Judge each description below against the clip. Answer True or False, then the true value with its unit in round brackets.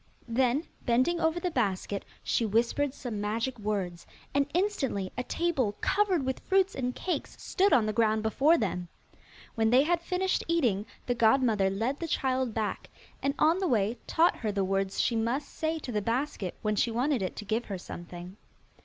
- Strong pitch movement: True (6.1 semitones)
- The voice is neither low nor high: False (240 Hz)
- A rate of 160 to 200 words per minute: True (185 wpm)